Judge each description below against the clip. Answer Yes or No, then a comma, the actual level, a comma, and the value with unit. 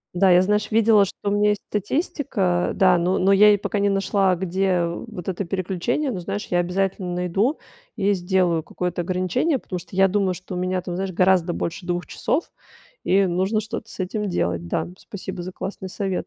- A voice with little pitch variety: Yes, narrow, 2.2 semitones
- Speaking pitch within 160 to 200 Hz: Yes, high, 190 Hz